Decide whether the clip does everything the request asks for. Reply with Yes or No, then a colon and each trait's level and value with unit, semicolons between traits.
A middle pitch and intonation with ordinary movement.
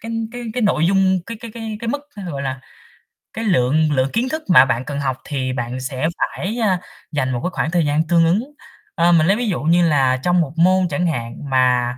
No: medium, 165 Hz; wide, 6.4 semitones